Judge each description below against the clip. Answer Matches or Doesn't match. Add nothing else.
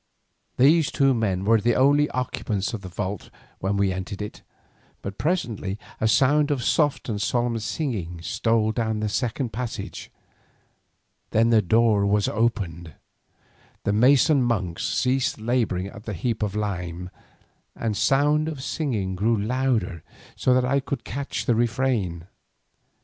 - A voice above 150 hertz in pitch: Doesn't match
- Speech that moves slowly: Doesn't match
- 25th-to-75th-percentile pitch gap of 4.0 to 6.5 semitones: Matches